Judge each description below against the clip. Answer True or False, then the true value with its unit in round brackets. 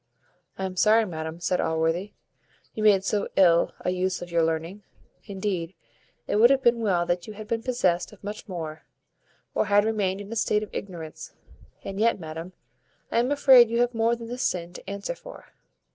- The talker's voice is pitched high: True (195 Hz)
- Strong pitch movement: False (4.4 semitones)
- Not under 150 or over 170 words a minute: False (195 wpm)